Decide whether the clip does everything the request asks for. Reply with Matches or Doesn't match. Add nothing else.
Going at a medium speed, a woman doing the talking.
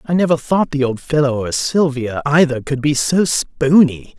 Doesn't match